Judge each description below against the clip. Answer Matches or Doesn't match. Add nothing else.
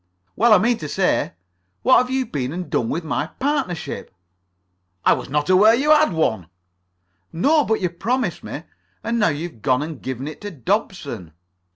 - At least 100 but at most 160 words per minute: Doesn't match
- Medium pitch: Matches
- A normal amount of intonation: Doesn't match